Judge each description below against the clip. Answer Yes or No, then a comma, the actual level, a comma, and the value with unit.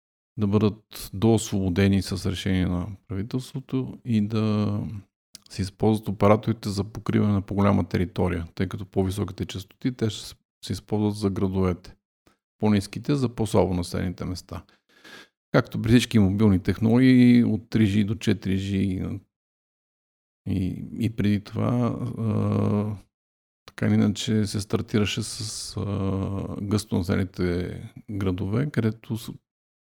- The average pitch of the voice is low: Yes, low, 105 Hz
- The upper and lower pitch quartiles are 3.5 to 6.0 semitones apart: No, narrow, 2.6 semitones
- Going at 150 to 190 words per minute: No, slow, 115 wpm